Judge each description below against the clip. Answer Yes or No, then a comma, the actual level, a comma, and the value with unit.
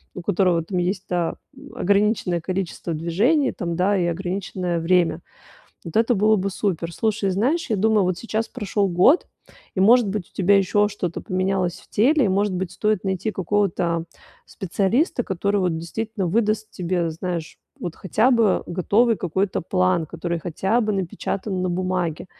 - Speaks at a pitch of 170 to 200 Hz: Yes, high, 190 Hz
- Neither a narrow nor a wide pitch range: Yes, average, 3.2 semitones